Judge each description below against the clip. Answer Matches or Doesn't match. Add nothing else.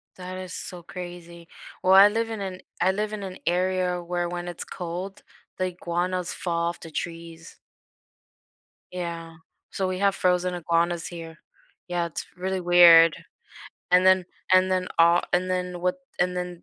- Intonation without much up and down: Matches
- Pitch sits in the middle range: Matches